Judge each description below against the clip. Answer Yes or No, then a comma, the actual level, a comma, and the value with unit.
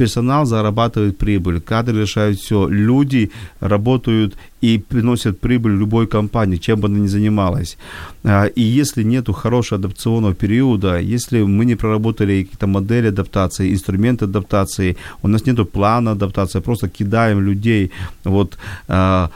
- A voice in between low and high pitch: No, low, 105 Hz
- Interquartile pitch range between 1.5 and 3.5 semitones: Yes, narrow, 2.6 semitones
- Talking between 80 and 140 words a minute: Yes, average, 130 wpm